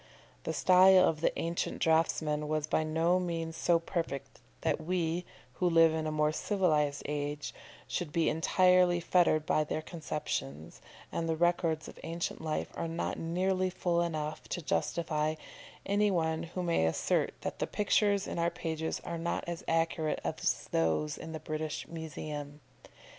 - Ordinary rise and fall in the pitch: No, narrow, 2.0 semitones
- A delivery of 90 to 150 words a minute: No, average, 160 wpm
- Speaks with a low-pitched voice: No, medium, 165 Hz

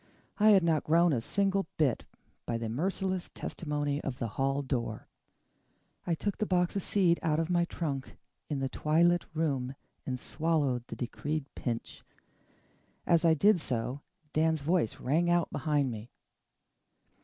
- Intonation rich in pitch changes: No, average, 4.4 semitones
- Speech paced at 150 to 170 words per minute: Yes, average, 155 wpm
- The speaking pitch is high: No, medium, 155 Hz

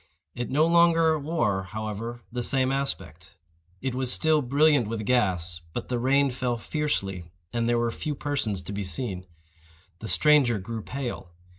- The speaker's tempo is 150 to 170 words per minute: Yes, average, 160 wpm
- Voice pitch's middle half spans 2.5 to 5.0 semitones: No, wide, 5.4 semitones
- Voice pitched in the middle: No, low, 120 Hz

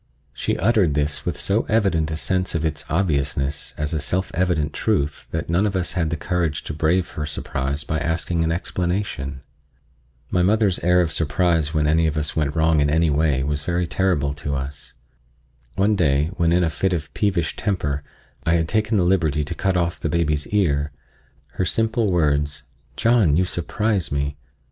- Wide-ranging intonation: No, average, 3.7 semitones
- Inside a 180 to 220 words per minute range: Yes, average, 185 wpm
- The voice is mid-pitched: No, very low, 80 Hz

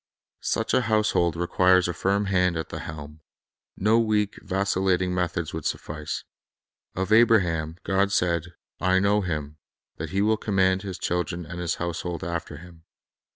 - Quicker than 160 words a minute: No, average, 155 wpm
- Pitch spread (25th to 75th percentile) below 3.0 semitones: Yes, narrow, 2.6 semitones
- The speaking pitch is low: Yes, very low, 90 Hz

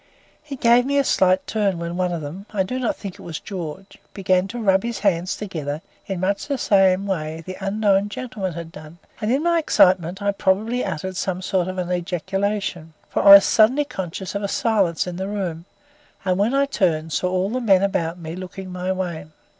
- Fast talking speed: Yes, fast, 210 wpm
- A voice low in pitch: No, high, 190 Hz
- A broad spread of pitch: No, average, 2.7 semitones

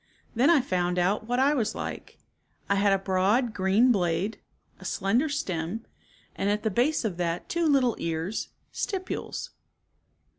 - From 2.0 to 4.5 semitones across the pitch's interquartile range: No, average, 5.3 semitones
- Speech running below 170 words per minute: Yes, average, 155 wpm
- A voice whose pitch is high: Yes, high, 210 Hz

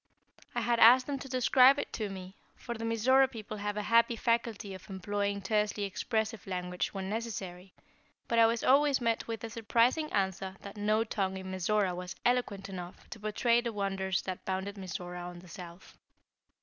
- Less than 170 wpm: No, average, 185 wpm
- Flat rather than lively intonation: No, average, 3.5 semitones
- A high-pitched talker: Yes, high, 210 Hz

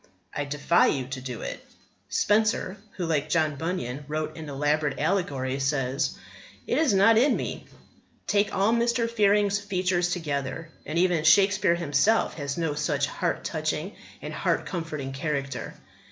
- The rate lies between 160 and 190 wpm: No, average, 150 wpm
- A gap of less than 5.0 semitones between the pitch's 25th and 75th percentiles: No, wide, 5.4 semitones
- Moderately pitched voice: Yes, medium, 160 Hz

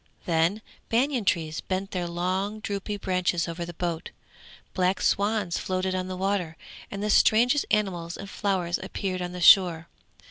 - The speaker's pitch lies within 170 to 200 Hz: Yes, medium, 185 Hz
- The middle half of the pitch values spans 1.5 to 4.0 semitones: Yes, narrow, 2.6 semitones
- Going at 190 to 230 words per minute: No, average, 155 wpm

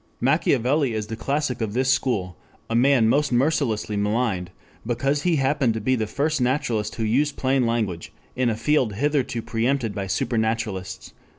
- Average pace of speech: Yes, average, 165 wpm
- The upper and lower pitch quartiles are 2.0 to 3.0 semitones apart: No, average, 3.9 semitones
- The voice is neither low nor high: No, low, 120 Hz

